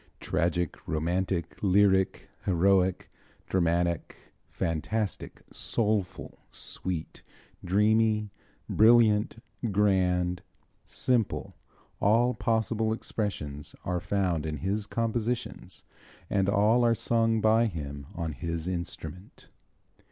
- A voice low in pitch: Yes, very low, 95 Hz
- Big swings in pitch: No, average, 4.0 semitones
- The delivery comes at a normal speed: No, slow, 85 wpm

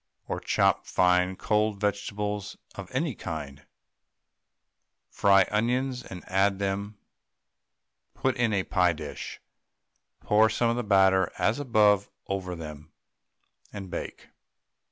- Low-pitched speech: Yes, low, 100 Hz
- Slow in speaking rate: Yes, slow, 120 wpm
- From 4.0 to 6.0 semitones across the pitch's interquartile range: No, narrow, 2.5 semitones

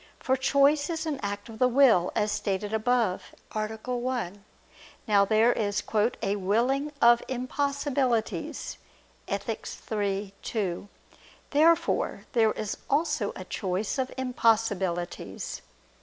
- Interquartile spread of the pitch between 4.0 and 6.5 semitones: Yes, average, 4.4 semitones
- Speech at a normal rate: No, slow, 115 wpm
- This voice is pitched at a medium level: No, high, 225 Hz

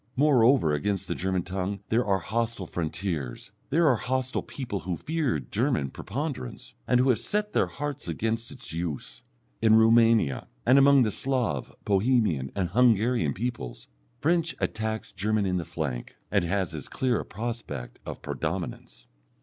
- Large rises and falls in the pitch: Yes, wide, 6.3 semitones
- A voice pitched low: Yes, low, 110 Hz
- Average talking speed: Yes, average, 155 wpm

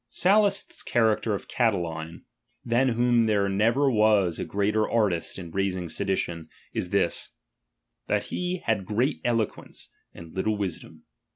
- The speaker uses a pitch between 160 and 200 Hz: No, low, 105 Hz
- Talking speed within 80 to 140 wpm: Yes, slow, 135 wpm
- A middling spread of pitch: Yes, average, 4.1 semitones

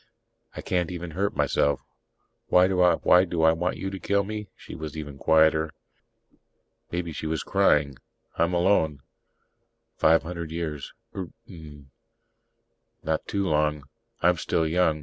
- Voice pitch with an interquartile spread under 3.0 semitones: Yes, narrow, 2.5 semitones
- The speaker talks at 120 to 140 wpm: Yes, slow, 135 wpm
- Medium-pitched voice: No, very low, 80 Hz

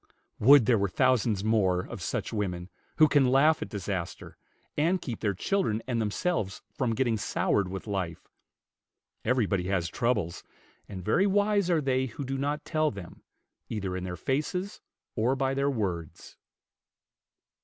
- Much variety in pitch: Yes, wide, 6.3 semitones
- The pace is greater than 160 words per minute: No, average, 155 wpm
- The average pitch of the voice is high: No, low, 115 Hz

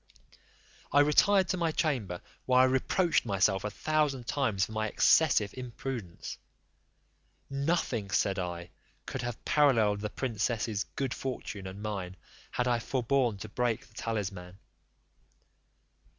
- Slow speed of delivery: Yes, slow, 130 wpm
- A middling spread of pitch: Yes, average, 4.9 semitones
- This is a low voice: Yes, low, 115 Hz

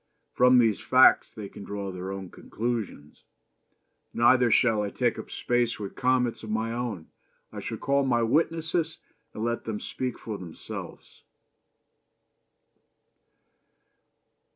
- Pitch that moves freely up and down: No, average, 3.4 semitones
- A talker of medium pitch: No, low, 115 Hz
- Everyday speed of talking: No, slow, 130 wpm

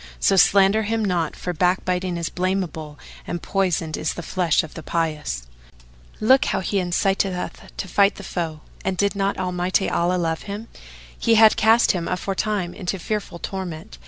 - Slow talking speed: No, average, 170 wpm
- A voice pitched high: No, medium, 180 Hz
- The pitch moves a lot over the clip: No, average, 2.8 semitones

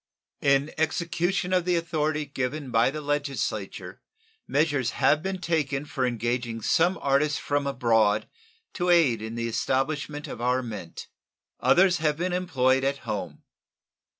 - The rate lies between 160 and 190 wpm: No, average, 140 wpm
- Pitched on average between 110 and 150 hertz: Yes, medium, 140 Hz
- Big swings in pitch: No, average, 4.5 semitones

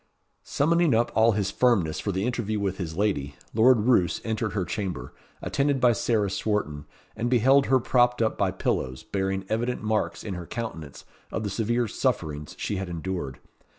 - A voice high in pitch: No, low, 105 Hz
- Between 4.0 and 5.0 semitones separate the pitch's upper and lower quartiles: Yes, average, 4.3 semitones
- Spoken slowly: No, average, 175 wpm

